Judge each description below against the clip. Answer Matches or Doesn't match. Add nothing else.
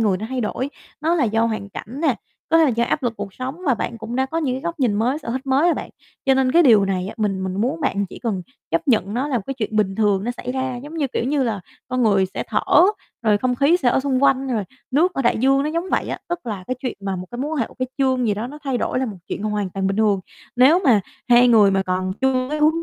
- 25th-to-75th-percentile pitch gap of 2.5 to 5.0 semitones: Matches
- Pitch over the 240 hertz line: Matches